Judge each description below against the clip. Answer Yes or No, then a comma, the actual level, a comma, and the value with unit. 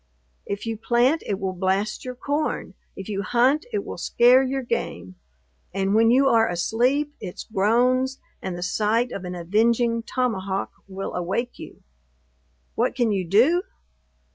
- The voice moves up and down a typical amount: Yes, average, 4.7 semitones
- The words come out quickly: No, average, 155 wpm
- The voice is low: No, high, 225 Hz